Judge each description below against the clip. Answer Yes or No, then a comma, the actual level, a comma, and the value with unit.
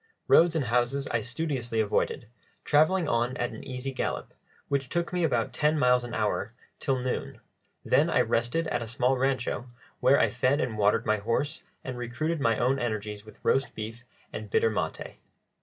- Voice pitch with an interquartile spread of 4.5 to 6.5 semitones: No, average, 3.3 semitones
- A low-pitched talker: Yes, low, 125 Hz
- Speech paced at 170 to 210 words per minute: Yes, average, 180 wpm